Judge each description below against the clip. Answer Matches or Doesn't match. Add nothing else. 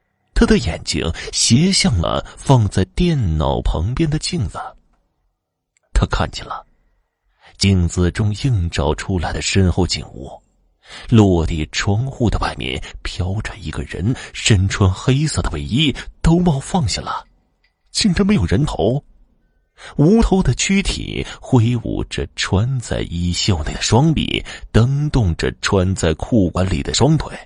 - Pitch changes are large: Matches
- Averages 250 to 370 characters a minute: Doesn't match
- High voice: Doesn't match